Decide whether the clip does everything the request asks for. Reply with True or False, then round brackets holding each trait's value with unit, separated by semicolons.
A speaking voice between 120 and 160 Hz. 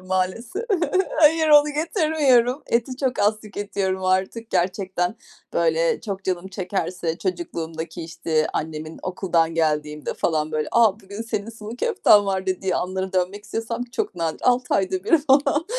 False (190 Hz)